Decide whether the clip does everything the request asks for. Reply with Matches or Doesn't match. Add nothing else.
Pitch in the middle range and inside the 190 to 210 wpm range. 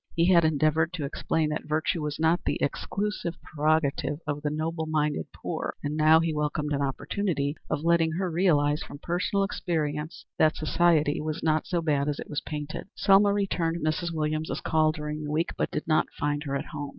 Matches